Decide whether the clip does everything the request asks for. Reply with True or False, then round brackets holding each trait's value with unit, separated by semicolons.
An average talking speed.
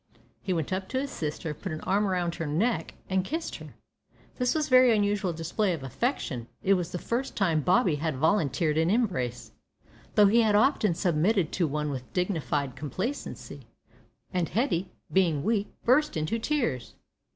True (175 wpm)